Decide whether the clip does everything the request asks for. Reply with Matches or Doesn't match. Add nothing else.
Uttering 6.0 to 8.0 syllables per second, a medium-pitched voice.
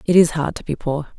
Matches